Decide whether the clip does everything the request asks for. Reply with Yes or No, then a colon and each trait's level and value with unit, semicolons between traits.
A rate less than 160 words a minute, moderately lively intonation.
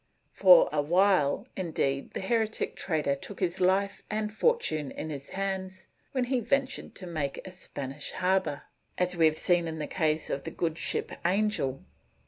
No: average, 165 wpm; average, 4.6 semitones